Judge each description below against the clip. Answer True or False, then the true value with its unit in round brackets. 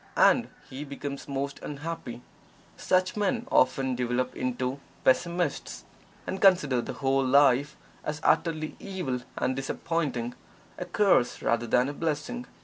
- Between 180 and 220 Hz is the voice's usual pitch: False (140 Hz)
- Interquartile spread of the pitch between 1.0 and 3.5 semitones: False (4.6 semitones)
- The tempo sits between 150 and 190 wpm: False (135 wpm)